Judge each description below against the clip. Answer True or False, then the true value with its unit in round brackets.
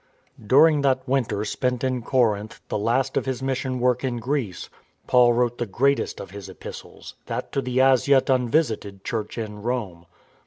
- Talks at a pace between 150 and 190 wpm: True (170 wpm)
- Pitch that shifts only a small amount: False (3.3 semitones)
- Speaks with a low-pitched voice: True (125 Hz)